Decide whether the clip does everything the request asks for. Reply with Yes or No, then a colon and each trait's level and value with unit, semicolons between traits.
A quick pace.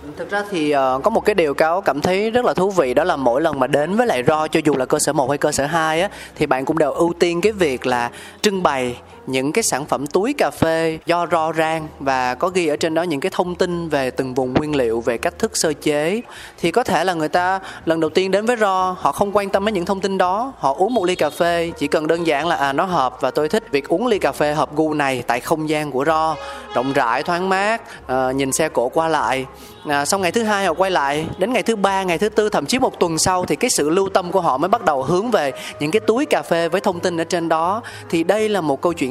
Yes: fast, 285 wpm